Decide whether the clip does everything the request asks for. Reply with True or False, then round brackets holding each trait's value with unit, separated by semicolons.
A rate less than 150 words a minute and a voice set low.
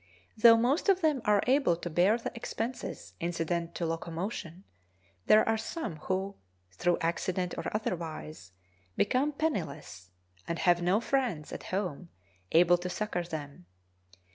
False (140 wpm; 180 Hz)